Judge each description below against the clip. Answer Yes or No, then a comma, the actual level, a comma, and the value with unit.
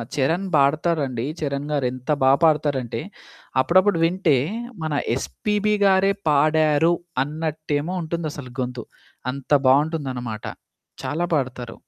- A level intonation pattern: No, average, 3.8 semitones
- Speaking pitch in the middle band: Yes, medium, 150 Hz